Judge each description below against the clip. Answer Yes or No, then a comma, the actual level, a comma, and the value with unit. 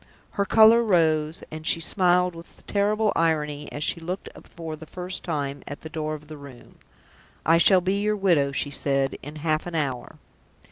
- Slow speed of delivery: No, average, 190 wpm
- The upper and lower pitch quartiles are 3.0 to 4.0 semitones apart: Yes, average, 3.5 semitones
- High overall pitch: No, medium, 160 Hz